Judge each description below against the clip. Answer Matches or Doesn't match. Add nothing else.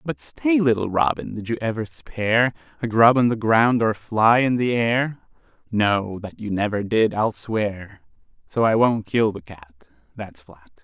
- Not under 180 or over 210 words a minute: Matches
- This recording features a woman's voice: Doesn't match